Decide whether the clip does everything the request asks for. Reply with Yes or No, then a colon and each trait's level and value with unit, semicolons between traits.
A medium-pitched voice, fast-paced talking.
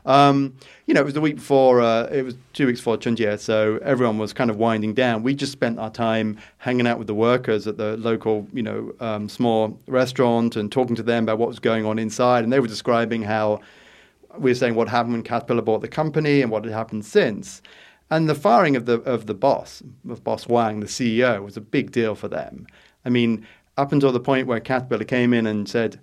No: low, 115 Hz; fast, 235 wpm